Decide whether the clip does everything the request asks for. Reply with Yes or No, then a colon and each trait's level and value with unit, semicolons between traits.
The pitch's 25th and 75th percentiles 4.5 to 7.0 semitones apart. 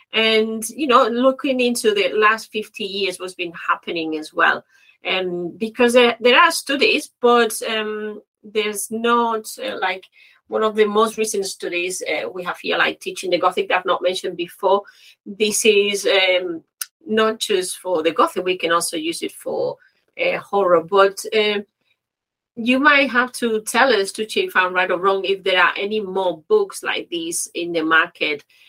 Yes: average, 4.9 semitones